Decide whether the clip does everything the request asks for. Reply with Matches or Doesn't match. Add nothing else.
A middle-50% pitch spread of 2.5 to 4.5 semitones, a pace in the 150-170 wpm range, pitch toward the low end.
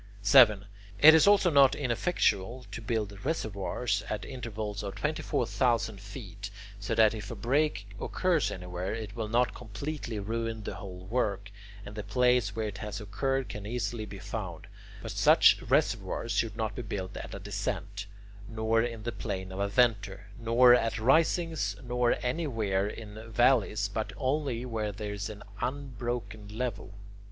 Matches